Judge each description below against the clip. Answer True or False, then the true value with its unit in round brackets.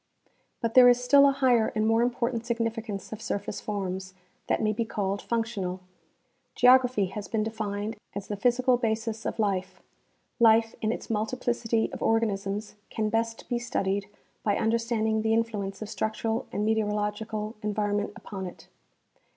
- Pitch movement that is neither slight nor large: False (2.0 semitones)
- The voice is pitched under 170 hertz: False (220 Hz)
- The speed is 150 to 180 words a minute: True (155 wpm)